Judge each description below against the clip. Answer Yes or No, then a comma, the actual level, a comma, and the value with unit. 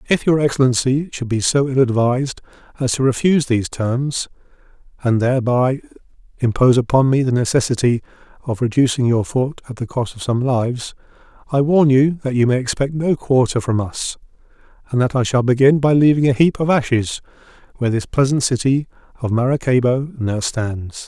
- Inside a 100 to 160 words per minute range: No, average, 170 wpm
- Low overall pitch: Yes, low, 130 Hz